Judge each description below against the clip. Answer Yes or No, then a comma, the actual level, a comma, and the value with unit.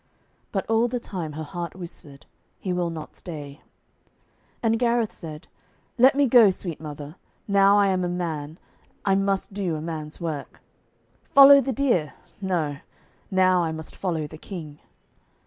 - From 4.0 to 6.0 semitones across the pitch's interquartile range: Yes, average, 4.3 semitones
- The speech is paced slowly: No, average, 155 wpm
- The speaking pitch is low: No, medium, 180 Hz